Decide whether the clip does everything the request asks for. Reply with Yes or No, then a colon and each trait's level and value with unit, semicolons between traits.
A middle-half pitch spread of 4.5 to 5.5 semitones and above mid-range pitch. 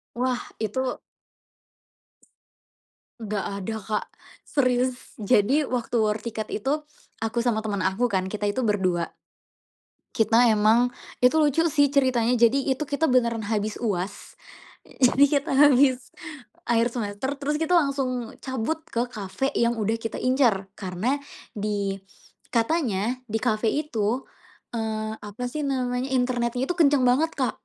No: average, 3.5 semitones; high, 240 Hz